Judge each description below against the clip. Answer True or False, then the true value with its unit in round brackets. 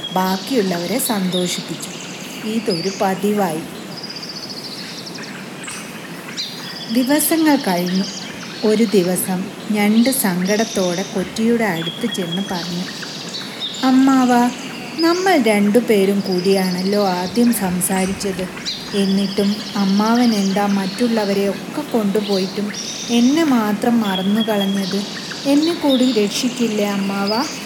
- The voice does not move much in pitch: False (3.5 semitones)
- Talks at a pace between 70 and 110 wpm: True (75 wpm)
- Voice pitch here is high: True (205 Hz)